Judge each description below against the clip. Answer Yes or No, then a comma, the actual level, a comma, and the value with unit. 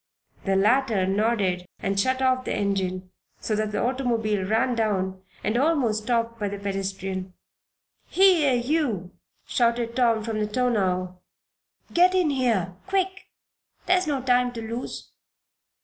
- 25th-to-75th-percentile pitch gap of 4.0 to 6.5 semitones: Yes, average, 4.8 semitones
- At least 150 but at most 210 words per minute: No, slow, 135 wpm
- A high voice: Yes, high, 225 Hz